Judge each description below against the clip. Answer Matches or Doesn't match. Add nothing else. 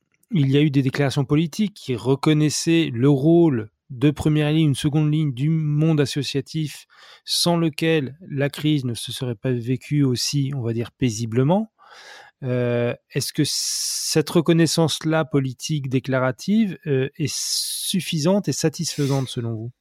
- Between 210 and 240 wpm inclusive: Doesn't match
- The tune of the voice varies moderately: Matches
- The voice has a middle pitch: Matches